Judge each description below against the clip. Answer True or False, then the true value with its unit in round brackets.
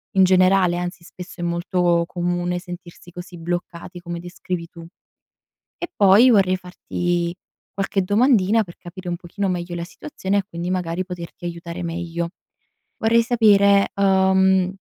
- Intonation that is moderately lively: False (1.9 semitones)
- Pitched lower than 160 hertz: False (180 Hz)